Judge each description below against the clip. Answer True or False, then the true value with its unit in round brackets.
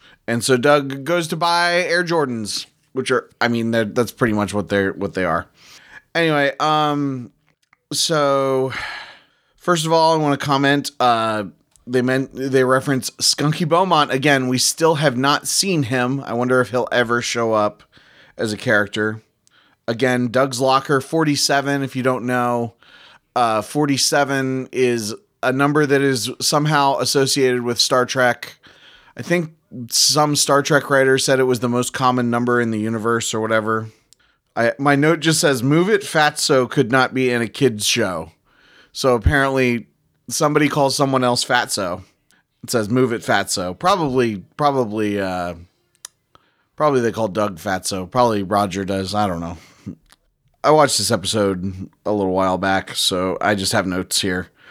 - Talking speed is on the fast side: False (160 wpm)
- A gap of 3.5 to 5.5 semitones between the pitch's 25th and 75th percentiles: True (4.3 semitones)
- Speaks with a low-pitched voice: True (125 Hz)